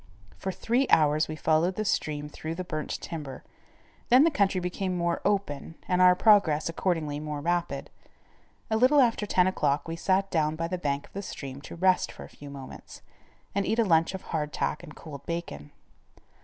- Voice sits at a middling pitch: Yes, medium, 170 Hz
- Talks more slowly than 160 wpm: No, average, 195 wpm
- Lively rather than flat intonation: No, average, 4.0 semitones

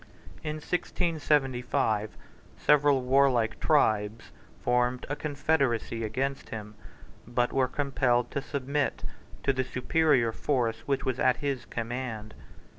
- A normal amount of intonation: Yes, average, 3.3 semitones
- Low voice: Yes, low, 130 Hz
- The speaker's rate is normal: No, slow, 115 wpm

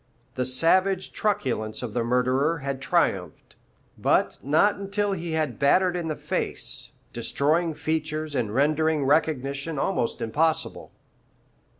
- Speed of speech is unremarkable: No, slow, 120 wpm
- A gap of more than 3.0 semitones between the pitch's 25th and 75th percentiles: Yes, average, 3.9 semitones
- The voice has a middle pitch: Yes, medium, 155 Hz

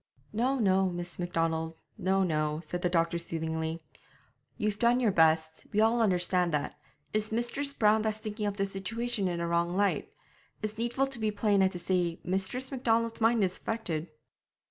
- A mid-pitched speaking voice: No, high, 195 Hz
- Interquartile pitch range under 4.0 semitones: No, average, 4.6 semitones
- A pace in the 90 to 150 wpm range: No, average, 180 wpm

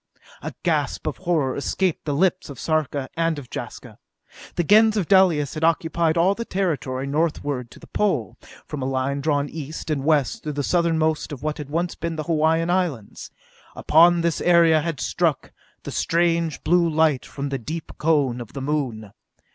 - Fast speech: No, average, 180 wpm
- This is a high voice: No, medium, 155 Hz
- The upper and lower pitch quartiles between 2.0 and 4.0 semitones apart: Yes, average, 3.1 semitones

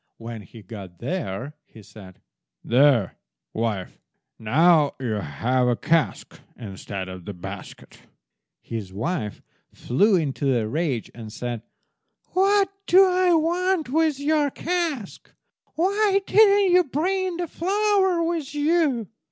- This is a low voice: No, medium, 175 Hz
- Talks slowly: Yes, slow, 125 wpm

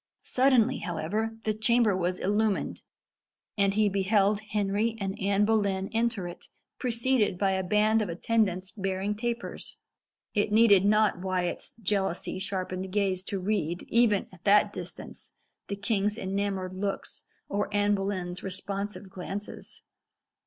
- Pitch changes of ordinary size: No, narrow, 2.1 semitones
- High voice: Yes, high, 200 Hz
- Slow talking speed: Yes, slow, 130 wpm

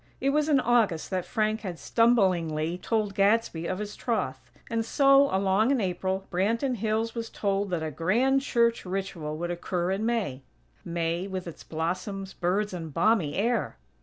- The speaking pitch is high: Yes, high, 195 Hz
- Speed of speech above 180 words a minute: No, average, 165 wpm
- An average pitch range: Yes, average, 4.7 semitones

